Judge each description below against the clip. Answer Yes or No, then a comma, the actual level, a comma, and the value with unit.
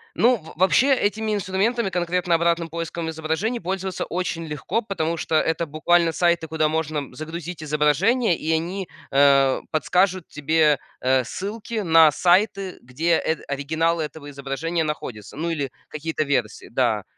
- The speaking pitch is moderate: Yes, medium, 165 Hz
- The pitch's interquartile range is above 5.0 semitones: No, average, 3.2 semitones